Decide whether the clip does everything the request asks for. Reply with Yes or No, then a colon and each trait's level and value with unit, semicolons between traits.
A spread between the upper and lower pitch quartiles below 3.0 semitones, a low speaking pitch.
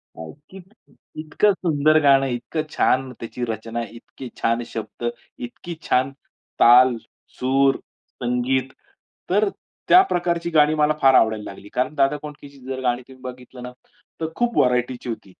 No: average, 3.8 semitones; low, 130 Hz